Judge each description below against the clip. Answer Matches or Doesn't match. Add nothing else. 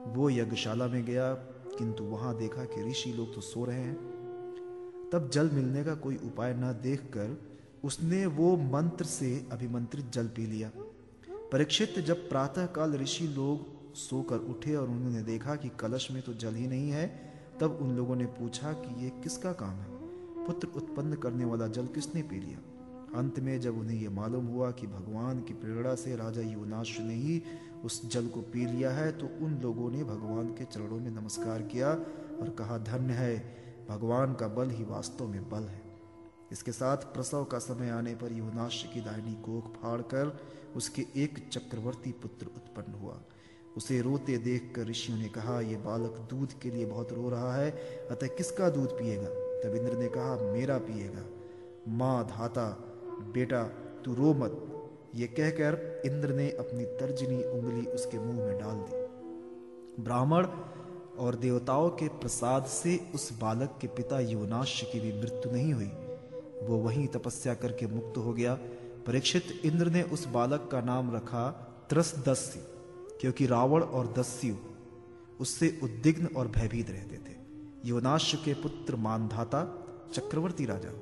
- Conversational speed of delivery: Matches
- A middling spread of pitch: Matches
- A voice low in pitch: Matches